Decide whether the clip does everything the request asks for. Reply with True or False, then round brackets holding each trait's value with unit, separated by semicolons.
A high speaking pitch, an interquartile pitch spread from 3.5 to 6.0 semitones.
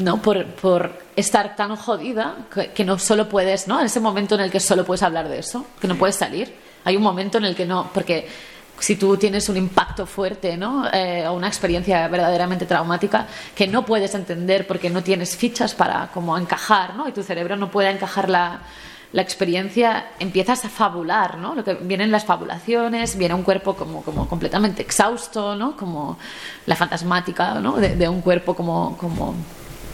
False (195 Hz; 2.9 semitones)